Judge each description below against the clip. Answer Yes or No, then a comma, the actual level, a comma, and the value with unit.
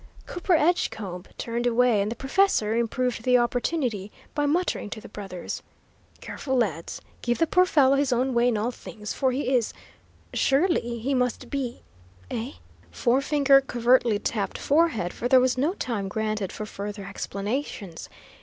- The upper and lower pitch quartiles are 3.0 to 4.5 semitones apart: Yes, average, 4.2 semitones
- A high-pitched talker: Yes, high, 245 Hz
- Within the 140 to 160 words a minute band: Yes, average, 155 wpm